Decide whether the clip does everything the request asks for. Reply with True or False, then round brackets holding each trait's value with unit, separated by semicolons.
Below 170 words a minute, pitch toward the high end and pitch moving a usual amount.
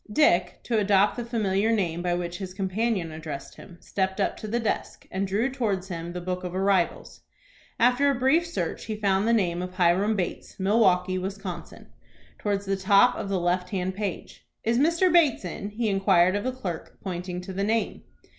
False (195 wpm; 195 Hz; 3.6 semitones)